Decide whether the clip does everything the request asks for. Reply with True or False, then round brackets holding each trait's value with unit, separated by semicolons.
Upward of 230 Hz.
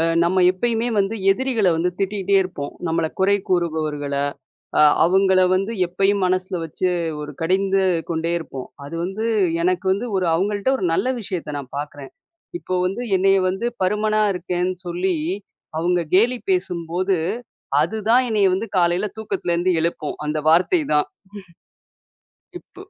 False (185 Hz)